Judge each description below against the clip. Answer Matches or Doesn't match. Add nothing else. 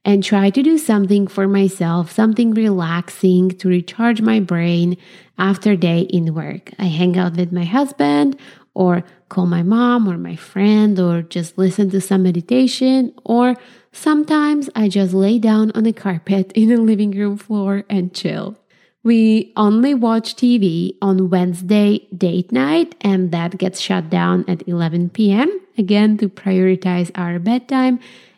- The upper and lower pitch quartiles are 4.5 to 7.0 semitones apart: Doesn't match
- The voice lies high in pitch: Matches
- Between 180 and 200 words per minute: Doesn't match